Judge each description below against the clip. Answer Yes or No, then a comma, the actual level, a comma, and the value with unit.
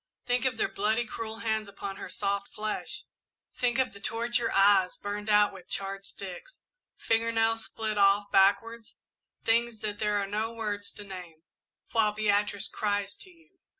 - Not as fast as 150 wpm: No, average, 165 wpm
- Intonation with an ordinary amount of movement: No, narrow, 2.1 semitones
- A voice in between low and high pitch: No, high, 210 Hz